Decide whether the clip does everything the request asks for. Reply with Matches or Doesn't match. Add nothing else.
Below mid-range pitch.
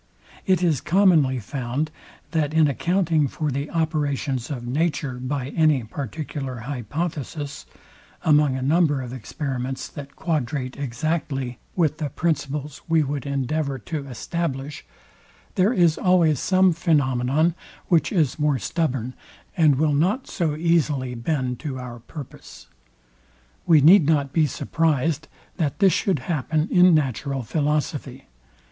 Doesn't match